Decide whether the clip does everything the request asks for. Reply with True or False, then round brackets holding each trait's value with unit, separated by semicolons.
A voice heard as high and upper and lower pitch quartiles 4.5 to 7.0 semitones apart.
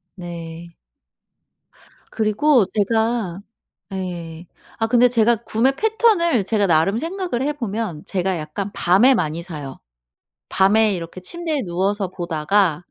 True (200 Hz; 5.6 semitones)